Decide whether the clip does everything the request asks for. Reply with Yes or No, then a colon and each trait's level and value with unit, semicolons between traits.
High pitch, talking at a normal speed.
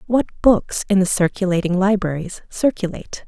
No: high, 195 Hz; slow, 130 wpm